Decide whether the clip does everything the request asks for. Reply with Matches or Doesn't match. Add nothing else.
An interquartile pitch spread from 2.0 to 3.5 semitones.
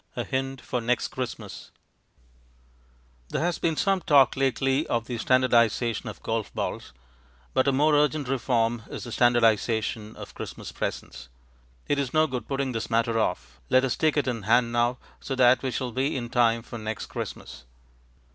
Matches